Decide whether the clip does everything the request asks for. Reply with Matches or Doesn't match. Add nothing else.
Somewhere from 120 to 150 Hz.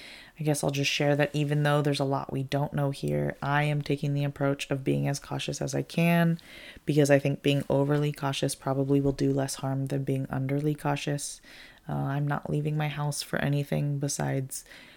Matches